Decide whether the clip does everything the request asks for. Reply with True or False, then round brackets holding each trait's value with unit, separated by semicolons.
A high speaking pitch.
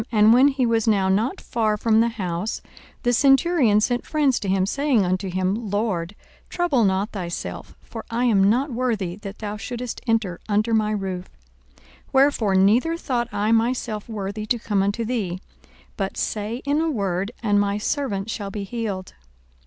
True (215 Hz)